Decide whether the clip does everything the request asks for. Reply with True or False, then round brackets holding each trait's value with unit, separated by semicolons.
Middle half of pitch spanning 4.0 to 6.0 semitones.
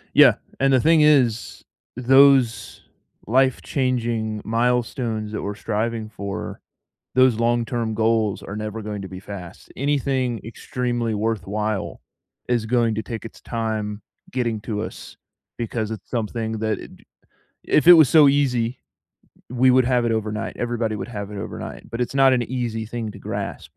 False (2.6 semitones)